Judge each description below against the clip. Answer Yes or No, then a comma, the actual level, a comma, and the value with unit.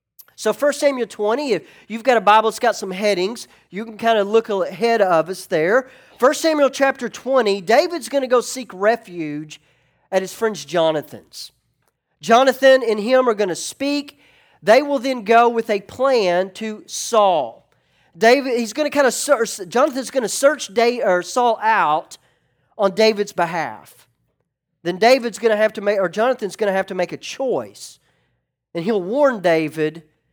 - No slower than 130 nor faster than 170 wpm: No, average, 180 wpm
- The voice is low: No, high, 220 Hz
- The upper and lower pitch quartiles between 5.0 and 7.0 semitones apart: Yes, average, 5.3 semitones